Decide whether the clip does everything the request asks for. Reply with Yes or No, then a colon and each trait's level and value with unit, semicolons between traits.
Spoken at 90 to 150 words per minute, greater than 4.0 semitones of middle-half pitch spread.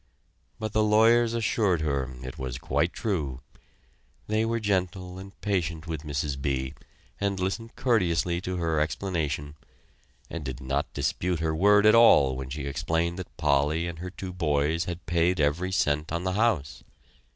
No: average, 165 wpm; average, 5.0 semitones